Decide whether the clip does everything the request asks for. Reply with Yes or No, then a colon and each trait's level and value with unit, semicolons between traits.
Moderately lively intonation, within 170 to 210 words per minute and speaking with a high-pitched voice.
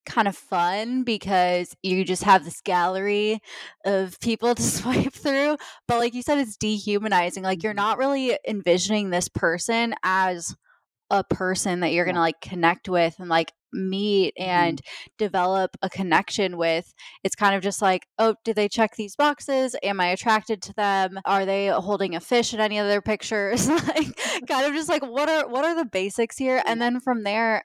Yes: average, 4.1 semitones; average, 185 wpm; high, 205 Hz